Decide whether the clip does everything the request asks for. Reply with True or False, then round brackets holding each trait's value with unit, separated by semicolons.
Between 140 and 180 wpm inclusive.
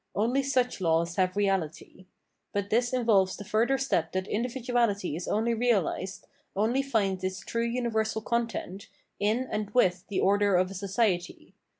True (160 wpm)